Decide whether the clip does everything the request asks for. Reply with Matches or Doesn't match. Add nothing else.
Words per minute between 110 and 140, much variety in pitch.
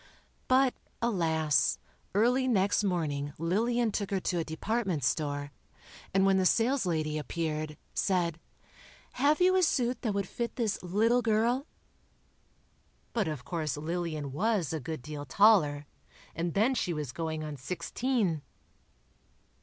Matches